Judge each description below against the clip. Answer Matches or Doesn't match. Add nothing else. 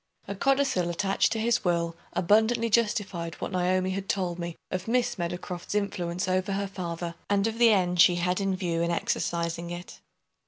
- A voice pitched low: Doesn't match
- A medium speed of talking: Matches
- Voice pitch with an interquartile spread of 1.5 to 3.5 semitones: Matches